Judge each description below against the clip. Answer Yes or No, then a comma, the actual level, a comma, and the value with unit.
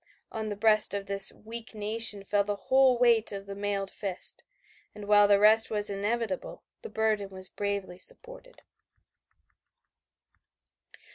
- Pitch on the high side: Yes, high, 205 Hz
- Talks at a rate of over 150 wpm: No, average, 140 wpm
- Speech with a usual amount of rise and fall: No, narrow, 1.9 semitones